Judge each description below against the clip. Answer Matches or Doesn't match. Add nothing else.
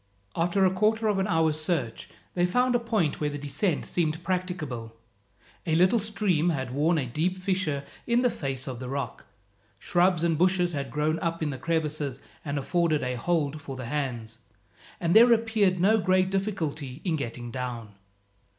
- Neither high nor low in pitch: Matches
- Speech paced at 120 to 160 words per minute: Doesn't match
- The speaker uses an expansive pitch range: Doesn't match